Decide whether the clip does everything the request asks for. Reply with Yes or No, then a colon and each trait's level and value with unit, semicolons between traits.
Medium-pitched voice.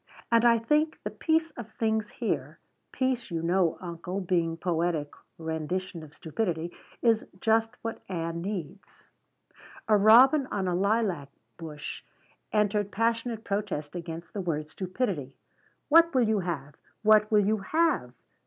No: high, 195 Hz